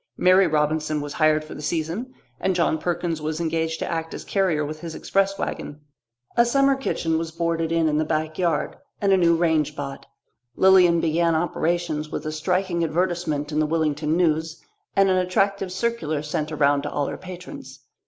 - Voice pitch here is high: No, medium, 165 Hz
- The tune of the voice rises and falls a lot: No, average, 2.9 semitones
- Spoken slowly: No, average, 185 wpm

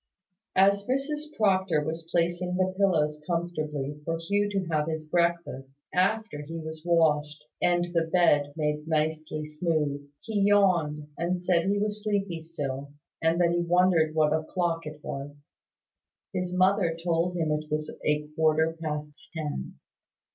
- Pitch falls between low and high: Yes, medium, 165 Hz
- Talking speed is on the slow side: No, average, 145 wpm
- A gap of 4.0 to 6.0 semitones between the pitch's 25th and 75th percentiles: No, average, 3.0 semitones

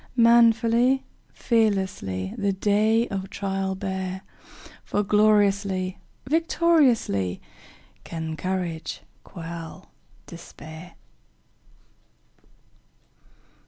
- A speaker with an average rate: No, slow, 60 wpm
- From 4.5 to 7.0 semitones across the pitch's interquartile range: No, average, 4.1 semitones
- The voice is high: Yes, high, 195 Hz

